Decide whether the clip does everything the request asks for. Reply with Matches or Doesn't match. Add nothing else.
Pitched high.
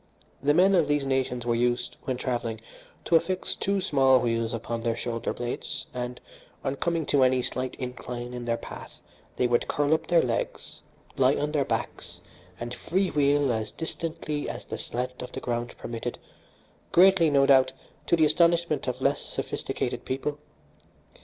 Doesn't match